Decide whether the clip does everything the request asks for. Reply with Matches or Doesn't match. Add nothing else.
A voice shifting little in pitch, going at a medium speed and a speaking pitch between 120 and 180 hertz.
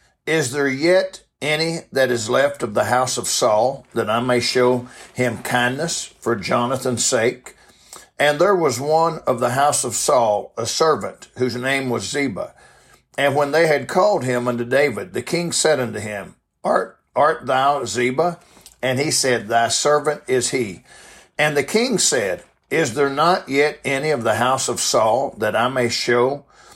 Doesn't match